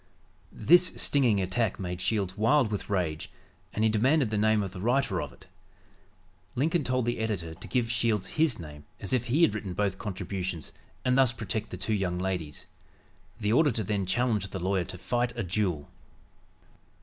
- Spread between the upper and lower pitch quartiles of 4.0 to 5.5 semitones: Yes, average, 4.4 semitones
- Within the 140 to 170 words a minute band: No, average, 180 wpm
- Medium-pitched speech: No, low, 105 Hz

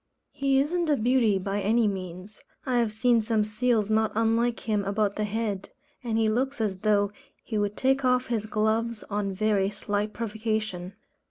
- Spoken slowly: No, average, 175 wpm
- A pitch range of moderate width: No, narrow, 2.3 semitones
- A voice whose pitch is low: No, high, 215 Hz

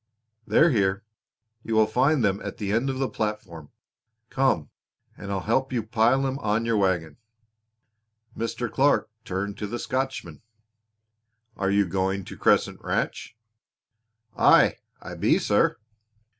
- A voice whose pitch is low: Yes, low, 110 Hz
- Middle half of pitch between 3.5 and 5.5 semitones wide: Yes, average, 4.6 semitones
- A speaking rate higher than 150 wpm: No, average, 140 wpm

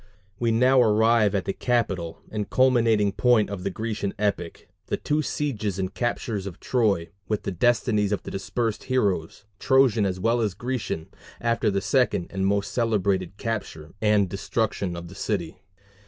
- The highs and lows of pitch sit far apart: No, average, 3.3 semitones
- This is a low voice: Yes, low, 105 Hz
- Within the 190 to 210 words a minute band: No, average, 165 wpm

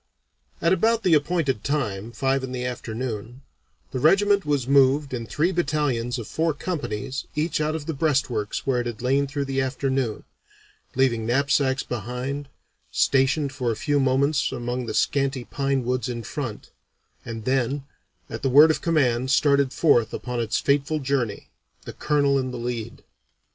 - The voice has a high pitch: No, low, 135 Hz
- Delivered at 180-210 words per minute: No, average, 165 wpm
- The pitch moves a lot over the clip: No, average, 3.0 semitones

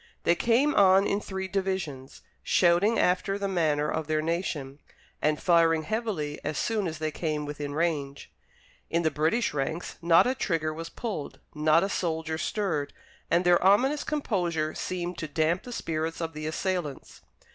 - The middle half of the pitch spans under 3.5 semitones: No, average, 3.8 semitones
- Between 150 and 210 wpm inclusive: Yes, average, 165 wpm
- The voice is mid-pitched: Yes, medium, 165 Hz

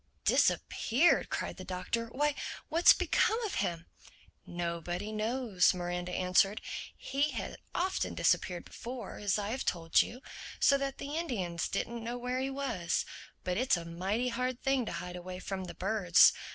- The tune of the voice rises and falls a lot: Yes, wide, 6.3 semitones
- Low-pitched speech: No, high, 215 Hz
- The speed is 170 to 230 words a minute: No, average, 160 wpm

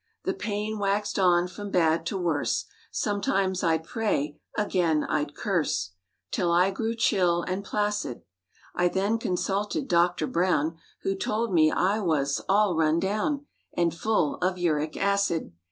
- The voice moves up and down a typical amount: Yes, average, 3.8 semitones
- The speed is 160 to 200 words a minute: No, average, 145 wpm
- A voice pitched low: No, medium, 185 Hz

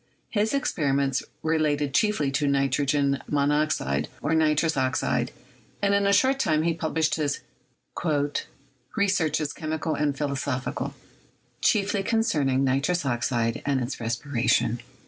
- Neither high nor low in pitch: Yes, medium, 145 Hz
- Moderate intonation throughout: Yes, average, 3.0 semitones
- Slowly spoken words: Yes, slow, 125 wpm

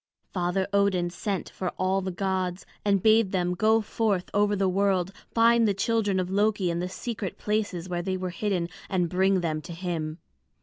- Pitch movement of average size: No, narrow, 2.3 semitones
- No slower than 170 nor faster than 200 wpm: Yes, average, 185 wpm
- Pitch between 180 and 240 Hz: Yes, high, 190 Hz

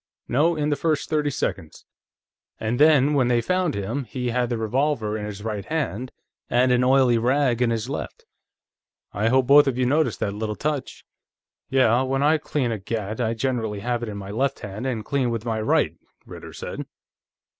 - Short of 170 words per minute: No, average, 195 wpm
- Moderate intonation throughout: Yes, average, 4.0 semitones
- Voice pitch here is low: Yes, low, 125 Hz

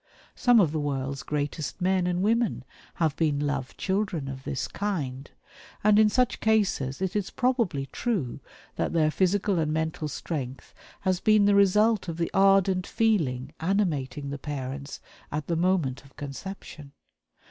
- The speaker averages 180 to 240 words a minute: No, average, 155 wpm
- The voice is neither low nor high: Yes, medium, 170 Hz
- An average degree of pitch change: No, wide, 5.9 semitones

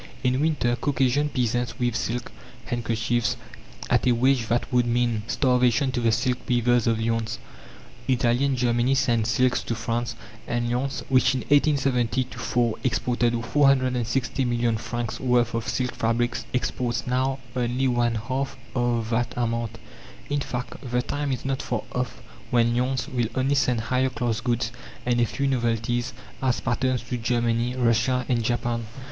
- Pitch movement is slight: Yes, narrow, 1.6 semitones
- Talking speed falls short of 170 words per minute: Yes, average, 155 wpm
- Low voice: Yes, low, 120 Hz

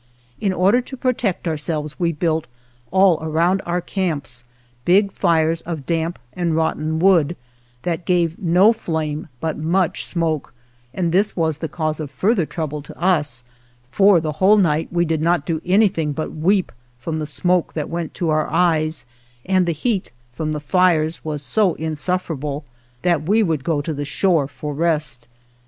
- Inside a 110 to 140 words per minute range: No, average, 170 wpm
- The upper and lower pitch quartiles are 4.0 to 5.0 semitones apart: No, average, 2.8 semitones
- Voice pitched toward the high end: No, medium, 165 Hz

